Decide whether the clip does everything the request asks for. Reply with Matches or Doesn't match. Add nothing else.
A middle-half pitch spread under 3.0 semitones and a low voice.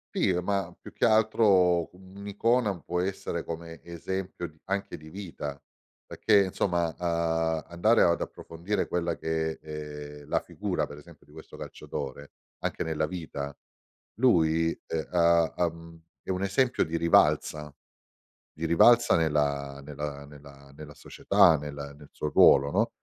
Doesn't match